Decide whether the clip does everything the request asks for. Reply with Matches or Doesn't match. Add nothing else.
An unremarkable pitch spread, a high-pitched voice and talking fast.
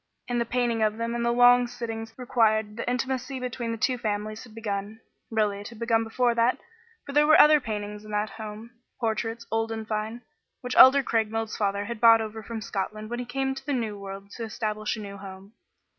Doesn't match